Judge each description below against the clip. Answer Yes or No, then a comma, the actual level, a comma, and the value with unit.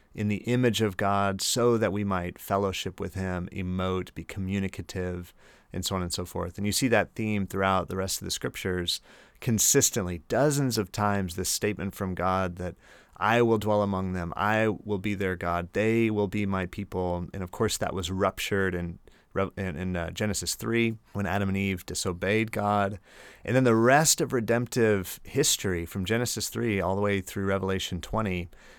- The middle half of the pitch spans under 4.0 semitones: Yes, average, 2.8 semitones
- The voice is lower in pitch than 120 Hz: Yes, low, 100 Hz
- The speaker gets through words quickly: No, average, 185 wpm